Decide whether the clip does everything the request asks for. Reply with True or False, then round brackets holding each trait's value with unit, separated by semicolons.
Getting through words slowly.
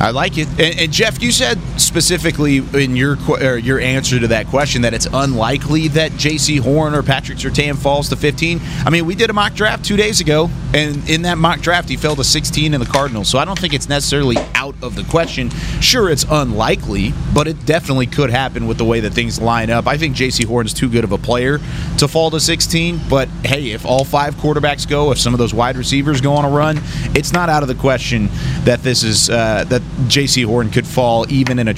False (235 wpm)